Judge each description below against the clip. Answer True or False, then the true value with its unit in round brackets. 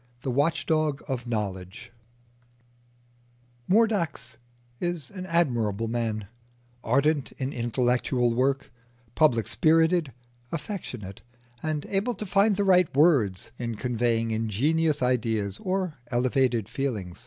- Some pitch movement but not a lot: False (6.0 semitones)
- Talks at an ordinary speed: False (110 wpm)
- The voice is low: True (130 Hz)